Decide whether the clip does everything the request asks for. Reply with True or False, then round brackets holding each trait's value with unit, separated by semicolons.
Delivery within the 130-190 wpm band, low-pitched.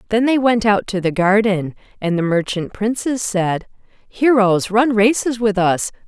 False (170 wpm; 210 Hz)